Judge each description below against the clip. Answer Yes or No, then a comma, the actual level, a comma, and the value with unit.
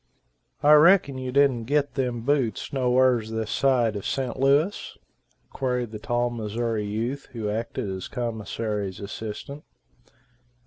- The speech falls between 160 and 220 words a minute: No, slow, 135 wpm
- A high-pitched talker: No, low, 120 Hz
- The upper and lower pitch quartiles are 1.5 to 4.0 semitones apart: Yes, average, 3.5 semitones